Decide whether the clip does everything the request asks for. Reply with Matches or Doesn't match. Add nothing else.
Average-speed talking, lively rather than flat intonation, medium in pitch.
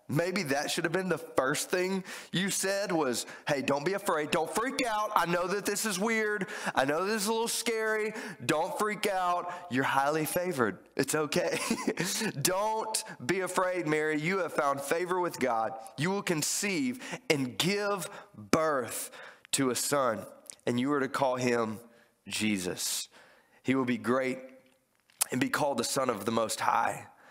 Matches